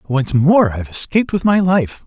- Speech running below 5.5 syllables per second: Yes, 5.2 syllables/s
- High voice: No, medium, 160 Hz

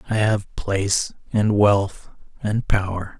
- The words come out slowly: Yes, slow, 130 wpm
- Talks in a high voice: No, low, 100 Hz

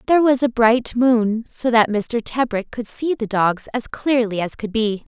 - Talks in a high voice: Yes, high, 230 Hz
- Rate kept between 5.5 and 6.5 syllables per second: No, 4.4 syllables/s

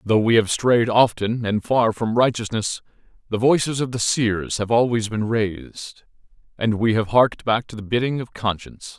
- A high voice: No, low, 110 Hz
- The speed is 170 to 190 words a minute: Yes, average, 185 wpm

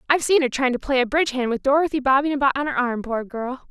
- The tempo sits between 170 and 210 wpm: No, fast, 275 wpm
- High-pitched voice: Yes, very high, 270 Hz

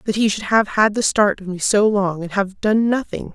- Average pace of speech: No, fast, 270 wpm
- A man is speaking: No, female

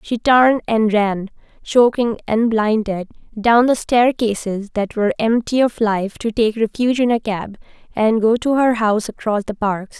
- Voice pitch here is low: No, high, 220 Hz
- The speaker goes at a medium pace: Yes, average, 175 wpm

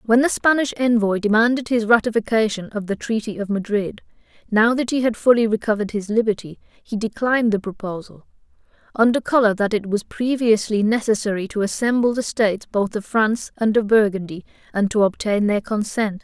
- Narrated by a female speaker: Yes, female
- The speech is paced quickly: No, average, 170 wpm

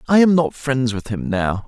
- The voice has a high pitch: No, low, 130 Hz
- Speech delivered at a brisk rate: Yes, fast, 250 wpm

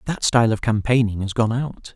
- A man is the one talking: Yes, male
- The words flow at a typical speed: No, fast, 215 wpm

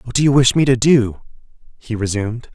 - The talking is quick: Yes, fast, 210 wpm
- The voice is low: Yes, low, 125 Hz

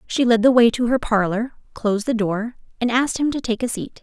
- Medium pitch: No, high, 230 Hz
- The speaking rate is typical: No, fast, 255 wpm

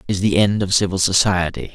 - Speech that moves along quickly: Yes, fast, 240 wpm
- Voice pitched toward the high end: No, very low, 95 Hz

